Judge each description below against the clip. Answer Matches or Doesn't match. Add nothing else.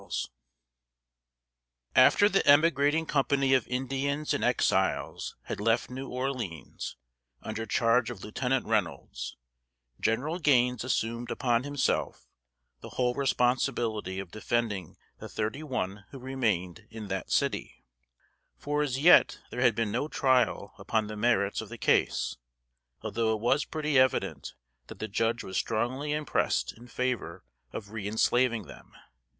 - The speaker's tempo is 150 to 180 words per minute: Doesn't match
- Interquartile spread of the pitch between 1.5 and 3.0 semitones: Doesn't match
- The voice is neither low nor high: Doesn't match